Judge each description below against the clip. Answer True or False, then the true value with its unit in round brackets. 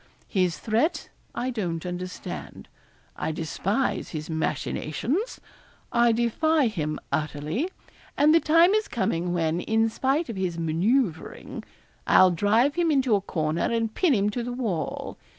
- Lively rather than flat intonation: True (7.6 semitones)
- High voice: True (215 Hz)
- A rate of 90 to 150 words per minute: True (140 wpm)